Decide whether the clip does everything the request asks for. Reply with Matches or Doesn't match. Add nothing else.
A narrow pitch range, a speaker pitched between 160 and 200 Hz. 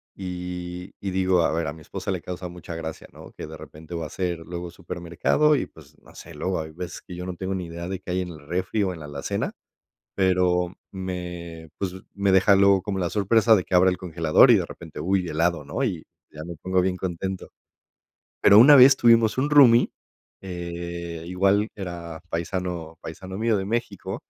Doesn't match